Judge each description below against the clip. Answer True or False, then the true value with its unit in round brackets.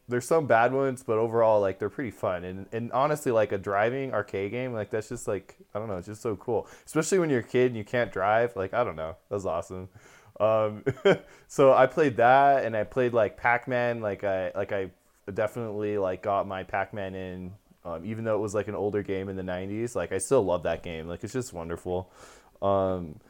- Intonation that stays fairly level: False (4.4 semitones)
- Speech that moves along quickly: True (225 wpm)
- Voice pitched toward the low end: True (105 Hz)